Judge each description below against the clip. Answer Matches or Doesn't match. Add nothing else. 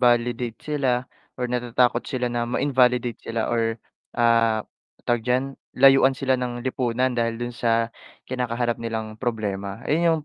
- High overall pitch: Doesn't match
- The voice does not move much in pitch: Matches